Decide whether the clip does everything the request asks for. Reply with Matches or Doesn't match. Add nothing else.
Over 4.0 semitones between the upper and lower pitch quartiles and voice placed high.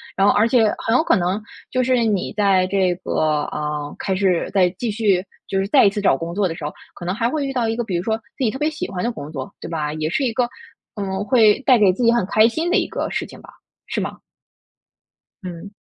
Matches